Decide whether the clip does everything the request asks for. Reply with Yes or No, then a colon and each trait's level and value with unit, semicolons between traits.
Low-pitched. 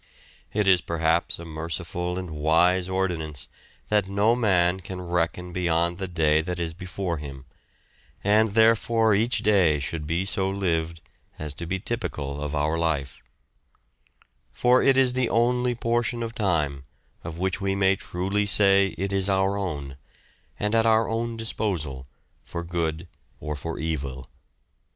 Yes: very low, 90 Hz